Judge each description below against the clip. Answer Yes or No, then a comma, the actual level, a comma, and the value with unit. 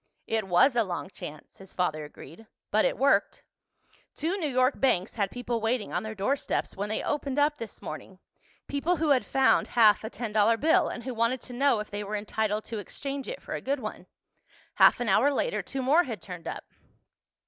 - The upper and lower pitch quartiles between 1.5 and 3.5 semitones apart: No, average, 4.8 semitones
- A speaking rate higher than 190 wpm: Yes, fast, 205 wpm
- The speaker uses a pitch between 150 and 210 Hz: No, high, 230 Hz